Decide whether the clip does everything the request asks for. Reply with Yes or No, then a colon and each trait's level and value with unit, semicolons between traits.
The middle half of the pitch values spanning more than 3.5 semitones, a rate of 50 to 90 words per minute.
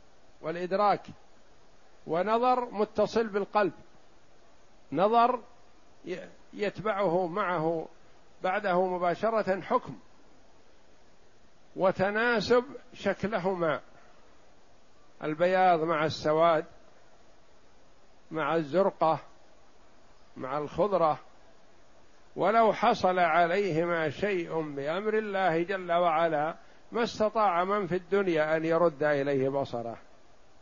Yes: average, 4.2 semitones; average, 70 wpm